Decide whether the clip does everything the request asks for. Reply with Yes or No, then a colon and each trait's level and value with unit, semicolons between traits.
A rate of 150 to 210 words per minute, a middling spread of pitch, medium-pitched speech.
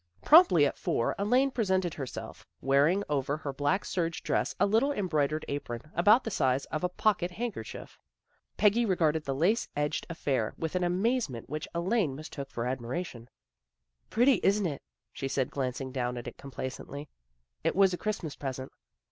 No: average, 175 wpm; wide, 6.5 semitones; medium, 155 Hz